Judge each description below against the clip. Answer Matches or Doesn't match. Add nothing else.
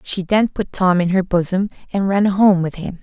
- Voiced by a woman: Matches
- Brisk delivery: Matches